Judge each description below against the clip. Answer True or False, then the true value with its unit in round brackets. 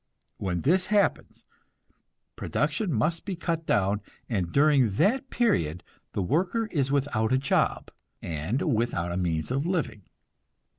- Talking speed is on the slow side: True (130 wpm)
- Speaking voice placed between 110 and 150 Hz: True (135 Hz)